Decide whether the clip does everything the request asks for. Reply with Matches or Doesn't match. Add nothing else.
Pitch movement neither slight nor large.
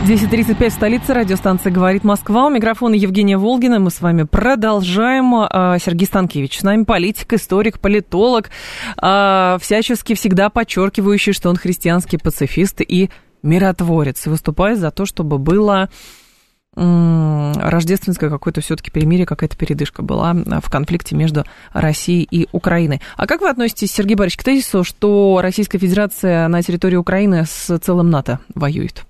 Matches